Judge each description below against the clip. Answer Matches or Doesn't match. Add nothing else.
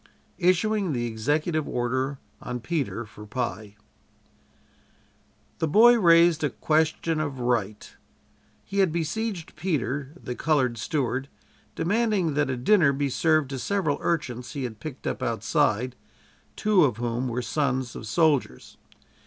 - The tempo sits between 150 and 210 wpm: Doesn't match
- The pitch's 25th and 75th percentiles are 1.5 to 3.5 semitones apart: Doesn't match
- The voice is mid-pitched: Matches